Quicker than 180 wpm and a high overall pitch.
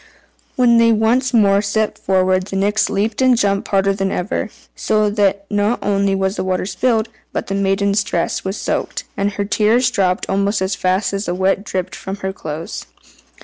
Yes: average, 190 wpm; high, 200 Hz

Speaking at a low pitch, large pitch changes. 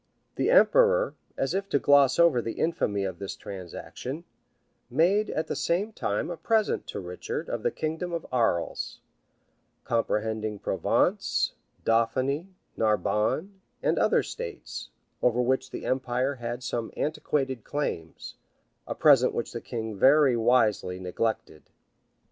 Yes: low, 130 Hz; wide, 6.1 semitones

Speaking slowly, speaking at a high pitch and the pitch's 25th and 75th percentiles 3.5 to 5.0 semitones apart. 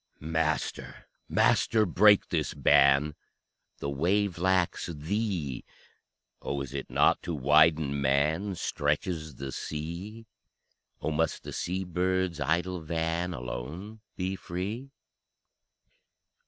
No: slow, 105 wpm; very low, 85 Hz; average, 4.2 semitones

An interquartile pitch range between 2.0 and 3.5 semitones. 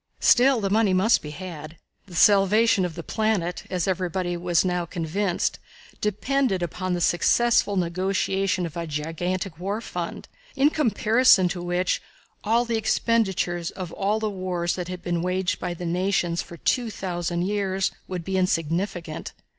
Yes: average, 2.8 semitones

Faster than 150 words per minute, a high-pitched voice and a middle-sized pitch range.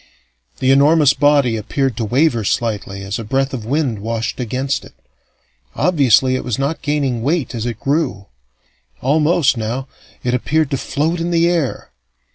No: average, 160 wpm; low, 135 Hz; average, 4.4 semitones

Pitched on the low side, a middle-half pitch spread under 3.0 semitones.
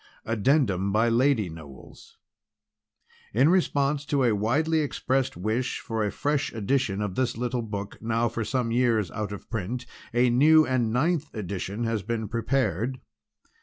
No: low, 115 Hz; average, 3.9 semitones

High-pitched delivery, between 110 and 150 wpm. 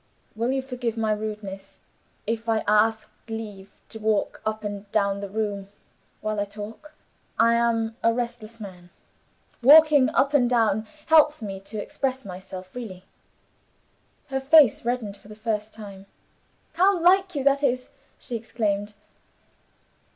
Yes: high, 220 Hz; average, 145 wpm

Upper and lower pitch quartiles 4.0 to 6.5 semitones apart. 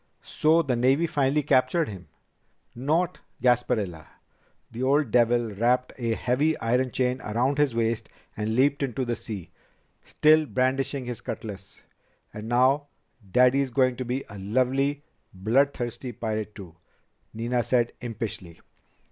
No: average, 3.2 semitones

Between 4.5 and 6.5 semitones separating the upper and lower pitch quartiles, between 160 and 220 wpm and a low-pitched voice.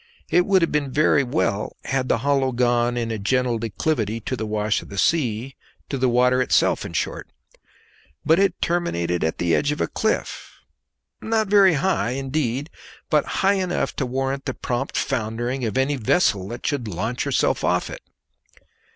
Yes: average, 4.8 semitones; average, 175 wpm; low, 130 Hz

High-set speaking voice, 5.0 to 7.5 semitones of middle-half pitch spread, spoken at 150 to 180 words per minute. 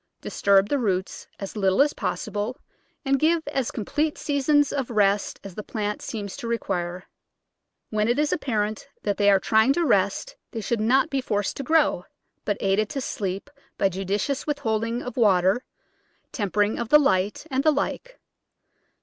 Yes: high, 220 Hz; wide, 5.4 semitones; average, 170 wpm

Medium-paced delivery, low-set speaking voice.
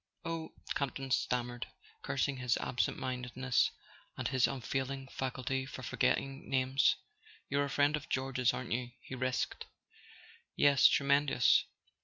No: slow, 125 wpm; low, 130 Hz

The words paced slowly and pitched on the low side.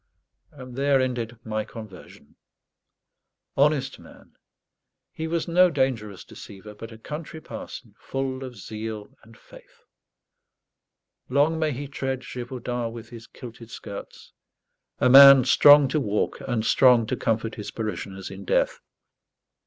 Yes: slow, 130 wpm; low, 125 Hz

